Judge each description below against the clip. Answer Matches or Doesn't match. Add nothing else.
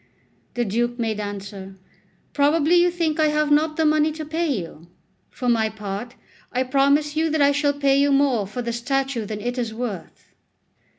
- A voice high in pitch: Matches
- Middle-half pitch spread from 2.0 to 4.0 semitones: Doesn't match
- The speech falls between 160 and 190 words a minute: Matches